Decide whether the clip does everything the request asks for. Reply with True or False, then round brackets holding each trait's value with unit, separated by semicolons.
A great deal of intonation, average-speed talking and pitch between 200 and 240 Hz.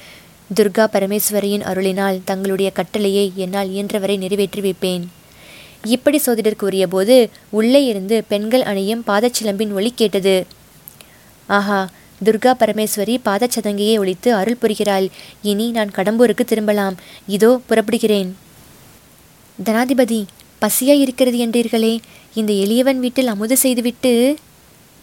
False (3.1 semitones; 100 wpm; 215 Hz)